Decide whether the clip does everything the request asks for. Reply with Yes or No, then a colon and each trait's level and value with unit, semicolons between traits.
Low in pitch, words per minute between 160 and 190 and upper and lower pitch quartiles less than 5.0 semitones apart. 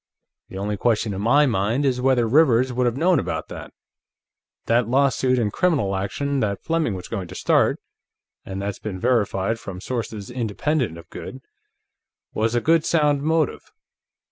No: low, 120 Hz; average, 165 wpm; wide, 5.4 semitones